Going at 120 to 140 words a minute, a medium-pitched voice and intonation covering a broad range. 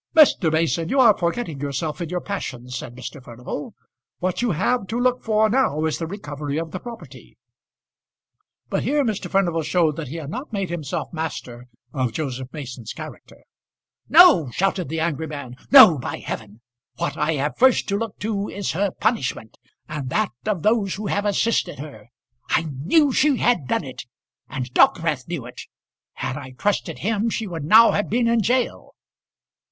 No: average, 180 wpm; medium, 170 Hz; wide, 7.0 semitones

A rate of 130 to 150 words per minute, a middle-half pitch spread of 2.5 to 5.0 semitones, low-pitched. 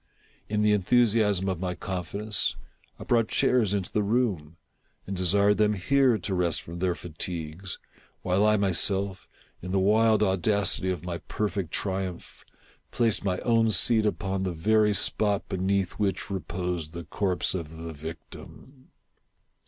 Yes: average, 145 wpm; average, 2.9 semitones; very low, 95 Hz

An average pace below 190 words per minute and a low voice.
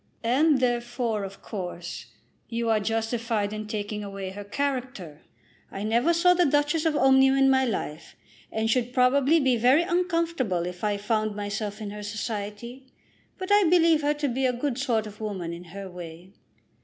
No: average, 175 wpm; high, 230 Hz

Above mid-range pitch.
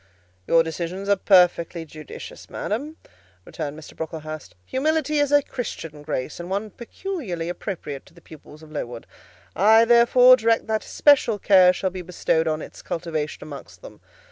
No: medium, 180 Hz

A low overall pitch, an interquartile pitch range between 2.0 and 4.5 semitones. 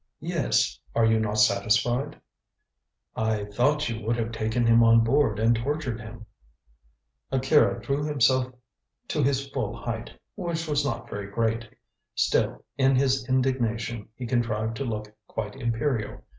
Yes: low, 115 Hz; average, 3.2 semitones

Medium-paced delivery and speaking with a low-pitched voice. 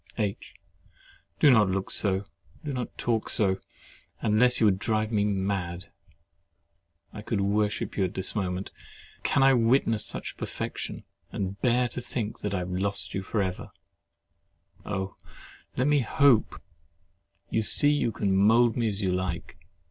Yes: average, 145 wpm; low, 105 Hz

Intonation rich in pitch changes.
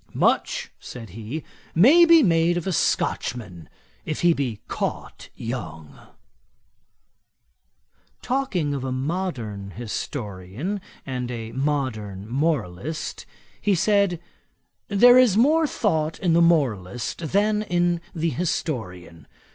Yes: wide, 8.3 semitones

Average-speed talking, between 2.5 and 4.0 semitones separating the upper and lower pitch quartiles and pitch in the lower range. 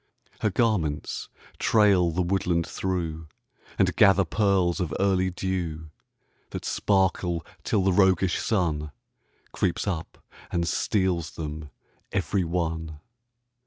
No: slow, 110 wpm; average, 2.8 semitones; very low, 90 Hz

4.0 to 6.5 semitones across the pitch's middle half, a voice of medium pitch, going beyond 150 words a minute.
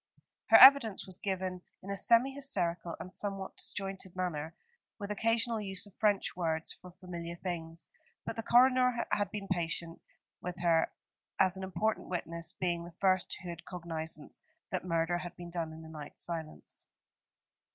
No: average, 3.1 semitones; medium, 180 Hz; average, 160 wpm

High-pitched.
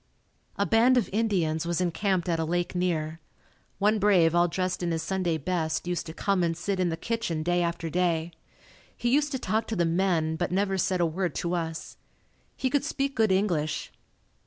No: medium, 175 Hz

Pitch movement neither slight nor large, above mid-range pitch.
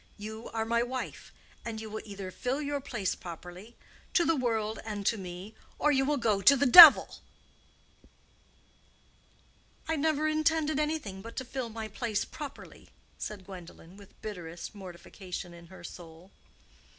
No: wide, 6.2 semitones; high, 220 Hz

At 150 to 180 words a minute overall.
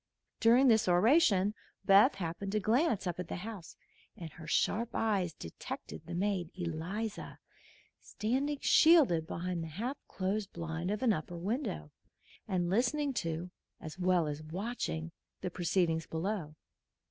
No: average, 140 wpm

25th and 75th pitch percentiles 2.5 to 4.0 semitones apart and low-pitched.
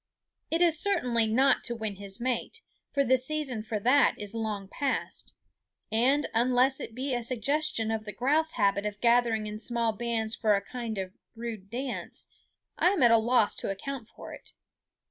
No: average, 3.4 semitones; high, 235 Hz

